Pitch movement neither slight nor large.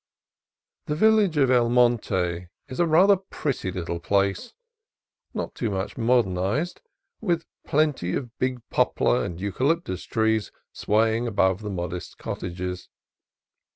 No: wide, 7.6 semitones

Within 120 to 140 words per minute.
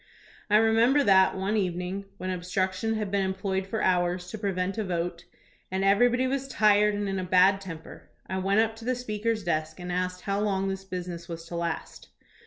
No: average, 200 wpm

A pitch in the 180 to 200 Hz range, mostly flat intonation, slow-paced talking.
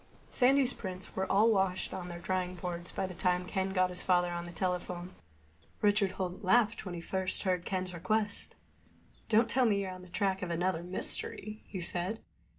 No: medium, 185 Hz; narrow, 2.1 semitones; average, 195 wpm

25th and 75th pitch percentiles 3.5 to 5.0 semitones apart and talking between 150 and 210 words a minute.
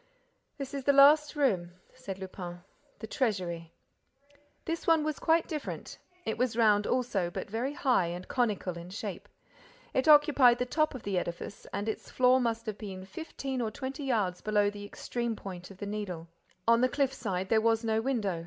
No: wide, 5.4 semitones; average, 185 wpm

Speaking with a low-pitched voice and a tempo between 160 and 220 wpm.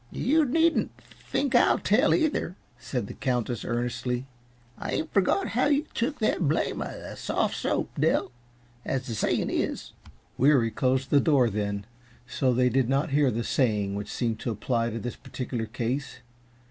Yes: low, 130 Hz; average, 170 wpm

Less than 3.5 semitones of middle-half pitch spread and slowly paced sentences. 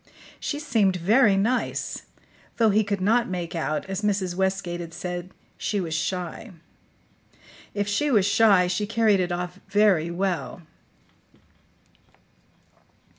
Yes: average, 2.9 semitones; slow, 125 wpm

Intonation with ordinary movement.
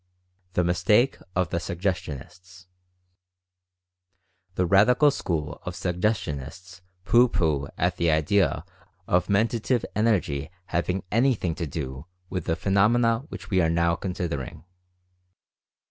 Yes: average, 3.5 semitones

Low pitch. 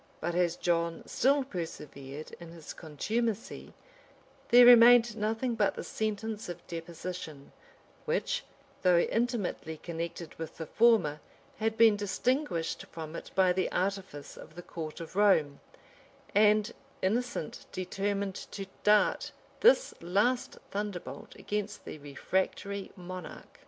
No: high, 190 Hz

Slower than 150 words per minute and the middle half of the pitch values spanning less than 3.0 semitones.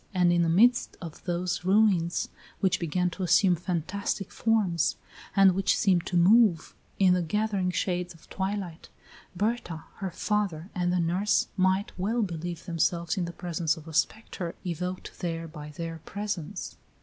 No: average, 160 wpm; narrow, 2.6 semitones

